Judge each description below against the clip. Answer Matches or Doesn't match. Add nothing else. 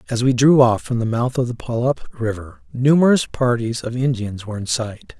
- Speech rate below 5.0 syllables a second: Doesn't match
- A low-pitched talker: Matches